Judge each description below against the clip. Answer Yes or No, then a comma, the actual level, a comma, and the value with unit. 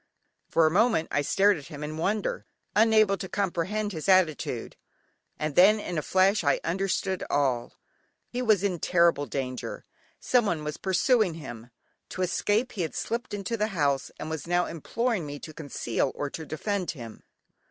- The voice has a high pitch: No, medium, 175 Hz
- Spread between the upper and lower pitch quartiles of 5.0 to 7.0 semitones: Yes, average, 5.3 semitones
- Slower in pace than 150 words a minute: No, average, 170 wpm